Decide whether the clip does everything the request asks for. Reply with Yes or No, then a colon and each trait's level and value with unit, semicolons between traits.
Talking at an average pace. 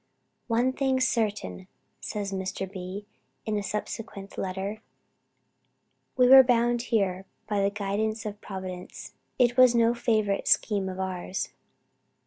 No: slow, 130 wpm